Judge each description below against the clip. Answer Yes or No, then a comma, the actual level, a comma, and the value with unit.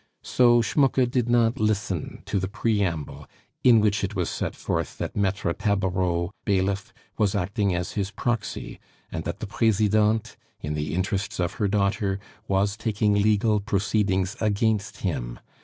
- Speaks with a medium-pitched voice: No, low, 100 Hz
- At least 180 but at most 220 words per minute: No, average, 150 wpm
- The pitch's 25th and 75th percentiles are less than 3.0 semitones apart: Yes, narrow, 2.4 semitones